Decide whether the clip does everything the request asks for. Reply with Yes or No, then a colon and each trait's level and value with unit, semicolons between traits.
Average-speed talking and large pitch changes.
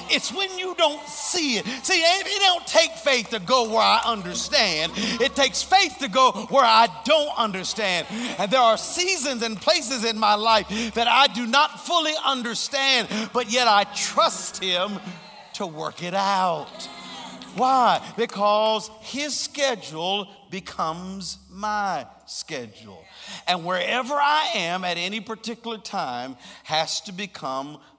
Yes: average, 145 wpm; wide, 5.9 semitones